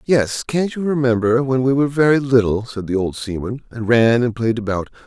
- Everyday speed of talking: No, fast, 215 wpm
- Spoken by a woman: No, male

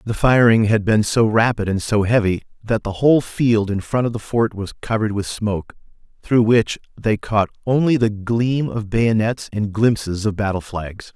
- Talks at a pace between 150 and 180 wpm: No, average, 195 wpm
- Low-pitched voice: Yes, low, 110 Hz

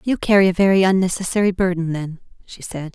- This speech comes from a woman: Yes, female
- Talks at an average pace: Yes, average, 185 wpm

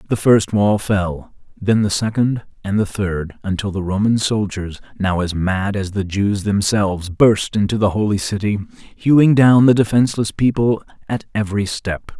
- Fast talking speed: No, average, 165 wpm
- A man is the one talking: Yes, male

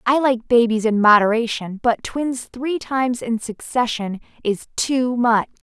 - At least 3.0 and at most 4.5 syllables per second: Yes, 4.2 syllables/s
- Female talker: Yes, female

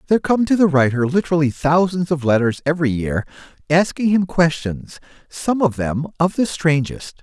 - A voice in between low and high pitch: Yes, medium, 160 Hz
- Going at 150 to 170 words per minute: Yes, average, 165 wpm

